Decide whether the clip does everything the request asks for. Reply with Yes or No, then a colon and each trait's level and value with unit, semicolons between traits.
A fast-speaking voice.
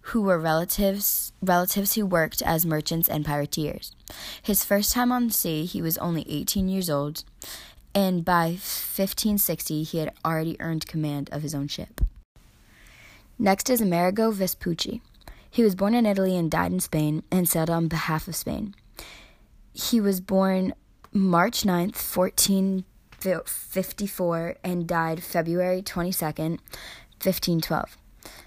No: average, 145 wpm